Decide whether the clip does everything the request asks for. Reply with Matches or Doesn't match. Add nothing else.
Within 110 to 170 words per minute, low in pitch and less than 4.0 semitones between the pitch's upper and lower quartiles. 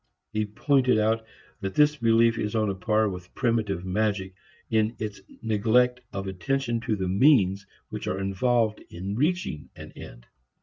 Matches